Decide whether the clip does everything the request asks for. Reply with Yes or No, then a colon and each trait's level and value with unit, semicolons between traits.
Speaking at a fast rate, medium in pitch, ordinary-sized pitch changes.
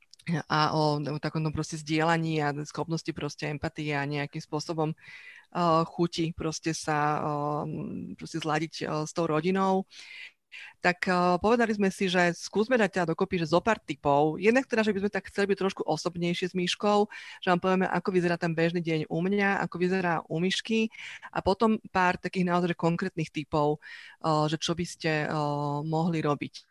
Yes: fast, 175 wpm; medium, 170 Hz; average, 3.2 semitones